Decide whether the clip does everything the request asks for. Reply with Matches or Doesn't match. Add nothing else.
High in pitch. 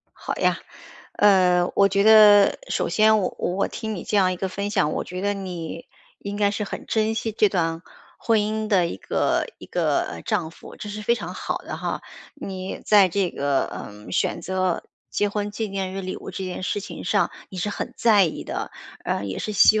Matches